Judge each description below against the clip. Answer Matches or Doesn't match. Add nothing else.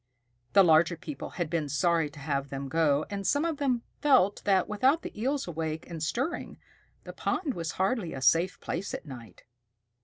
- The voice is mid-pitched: Matches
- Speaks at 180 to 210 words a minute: Matches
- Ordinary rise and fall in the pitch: Doesn't match